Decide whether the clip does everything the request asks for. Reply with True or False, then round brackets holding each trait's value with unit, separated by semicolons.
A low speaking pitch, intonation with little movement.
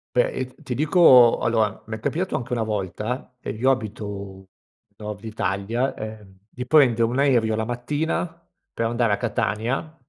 False (115 Hz; 3.3 semitones)